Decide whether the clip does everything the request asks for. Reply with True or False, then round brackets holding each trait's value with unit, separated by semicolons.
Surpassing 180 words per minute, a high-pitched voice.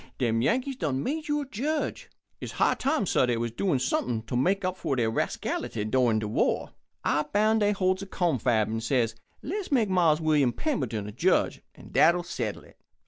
False (195 wpm; 155 Hz)